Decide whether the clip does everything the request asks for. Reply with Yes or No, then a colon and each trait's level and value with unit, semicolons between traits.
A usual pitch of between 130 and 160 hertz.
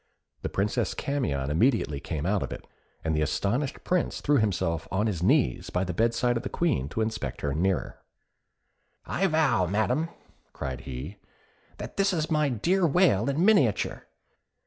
No: low, 110 Hz